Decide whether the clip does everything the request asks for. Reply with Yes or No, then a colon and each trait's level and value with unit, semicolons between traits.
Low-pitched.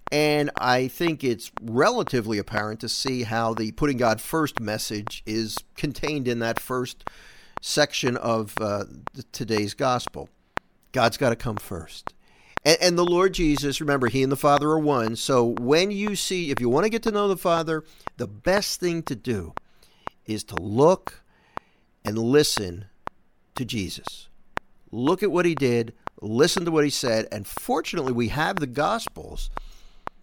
Yes: low, 130 Hz